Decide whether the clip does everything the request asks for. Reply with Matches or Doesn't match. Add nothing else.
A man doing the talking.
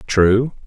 Matches